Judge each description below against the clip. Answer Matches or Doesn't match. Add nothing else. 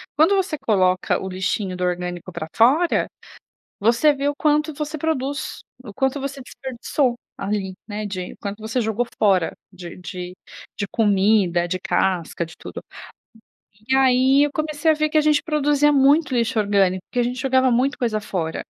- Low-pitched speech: Doesn't match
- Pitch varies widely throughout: Matches